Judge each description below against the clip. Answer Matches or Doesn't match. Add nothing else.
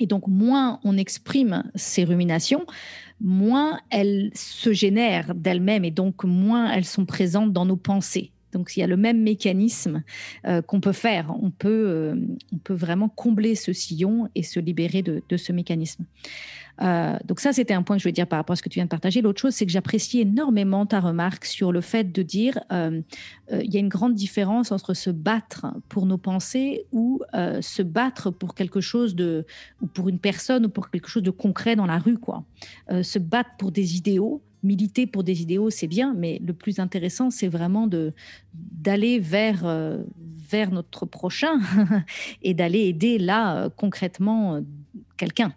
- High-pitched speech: Matches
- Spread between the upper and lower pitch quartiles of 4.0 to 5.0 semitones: Doesn't match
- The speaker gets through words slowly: Doesn't match